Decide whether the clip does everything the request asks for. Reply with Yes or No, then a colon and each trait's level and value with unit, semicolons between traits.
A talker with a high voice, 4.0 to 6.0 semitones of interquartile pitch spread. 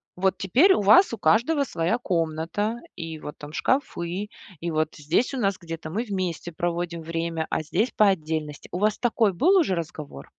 No: medium, 175 Hz; average, 4.9 semitones